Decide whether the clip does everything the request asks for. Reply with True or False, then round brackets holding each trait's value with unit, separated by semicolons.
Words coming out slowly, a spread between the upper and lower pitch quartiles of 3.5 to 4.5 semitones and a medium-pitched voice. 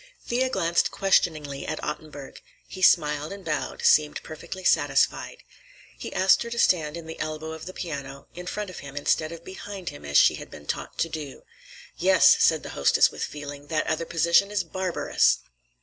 False (185 wpm; 3.9 semitones; 160 Hz)